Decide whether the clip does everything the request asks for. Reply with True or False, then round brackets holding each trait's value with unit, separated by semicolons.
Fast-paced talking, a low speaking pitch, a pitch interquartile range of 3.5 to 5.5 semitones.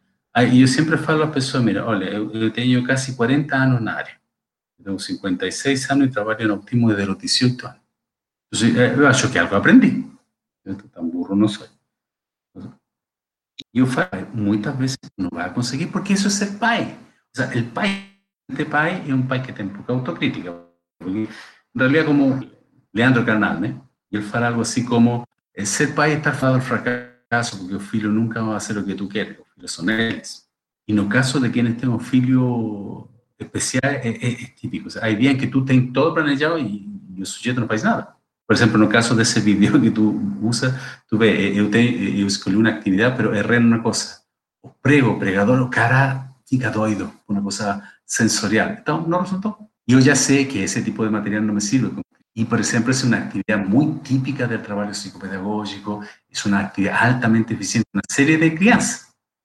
True (195 wpm; 120 Hz; 4.1 semitones)